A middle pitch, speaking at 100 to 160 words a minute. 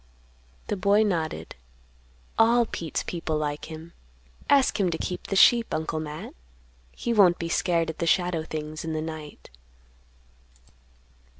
Yes: medium, 165 Hz; average, 140 wpm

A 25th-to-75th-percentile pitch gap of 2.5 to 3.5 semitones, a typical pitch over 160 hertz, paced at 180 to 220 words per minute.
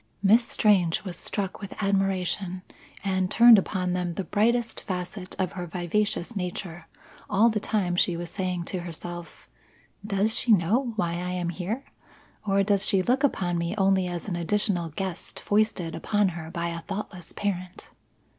No: average, 2.8 semitones; high, 190 Hz; average, 165 wpm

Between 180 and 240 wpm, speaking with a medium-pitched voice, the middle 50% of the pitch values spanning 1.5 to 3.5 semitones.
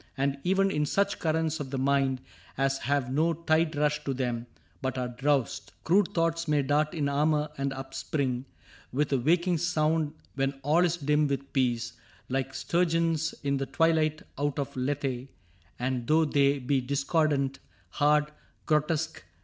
No: average, 155 wpm; medium, 145 Hz; average, 2.8 semitones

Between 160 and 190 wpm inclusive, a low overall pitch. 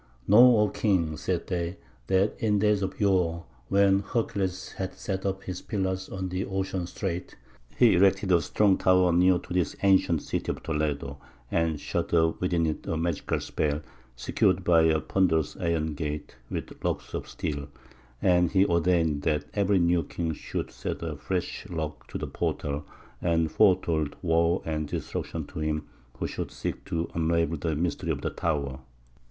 Yes: average, 170 wpm; very low, 85 Hz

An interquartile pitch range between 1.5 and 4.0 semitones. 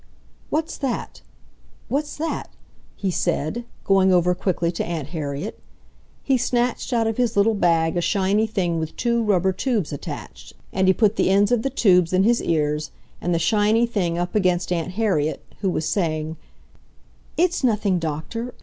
No: average, 5.2 semitones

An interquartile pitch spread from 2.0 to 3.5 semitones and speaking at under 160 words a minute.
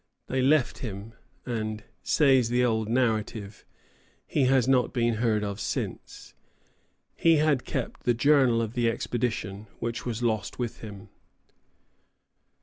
Yes: average, 2.7 semitones; slow, 135 wpm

